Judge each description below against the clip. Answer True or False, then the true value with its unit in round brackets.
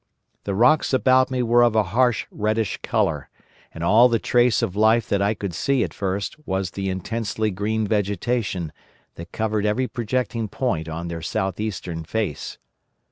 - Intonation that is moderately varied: True (3.7 semitones)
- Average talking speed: True (170 wpm)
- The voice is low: True (105 Hz)